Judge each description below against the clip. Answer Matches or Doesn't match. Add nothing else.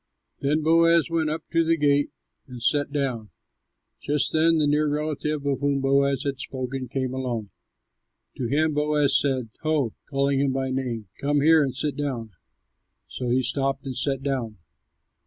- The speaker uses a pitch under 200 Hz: Matches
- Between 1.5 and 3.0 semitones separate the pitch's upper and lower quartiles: Matches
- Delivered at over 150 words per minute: Matches